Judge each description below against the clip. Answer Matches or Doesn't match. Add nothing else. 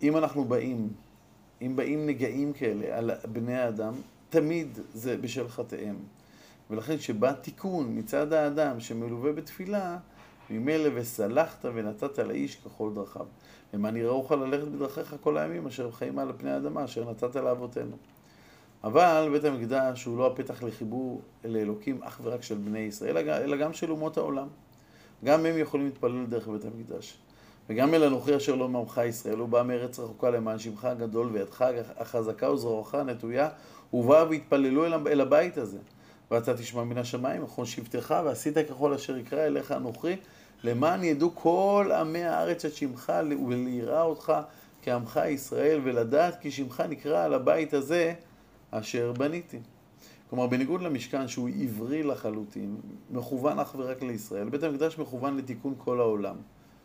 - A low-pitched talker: Matches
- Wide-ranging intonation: Doesn't match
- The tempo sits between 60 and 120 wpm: Doesn't match